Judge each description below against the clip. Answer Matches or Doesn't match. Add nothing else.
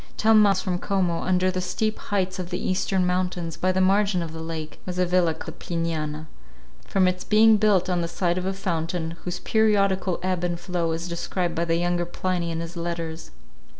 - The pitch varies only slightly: Matches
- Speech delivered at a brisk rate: Matches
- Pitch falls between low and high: Matches